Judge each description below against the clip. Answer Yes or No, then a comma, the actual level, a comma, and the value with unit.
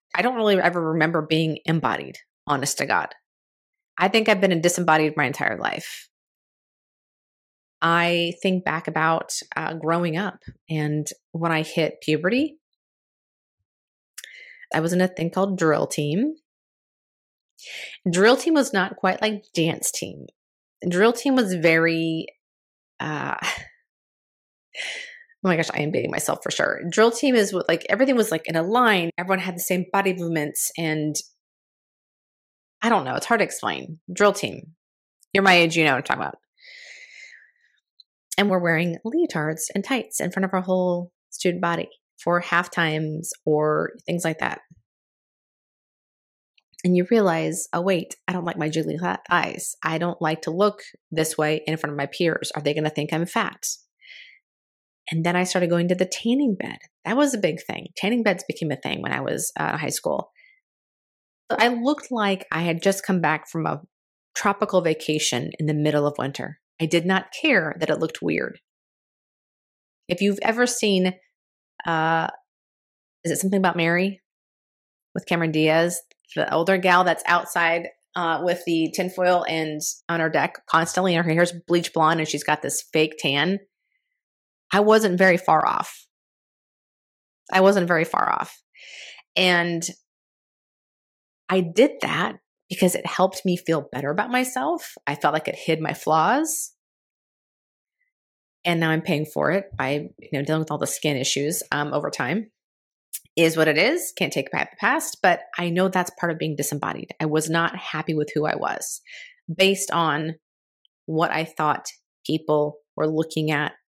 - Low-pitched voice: No, medium, 175 Hz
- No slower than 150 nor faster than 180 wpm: Yes, average, 170 wpm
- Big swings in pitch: No, average, 3.8 semitones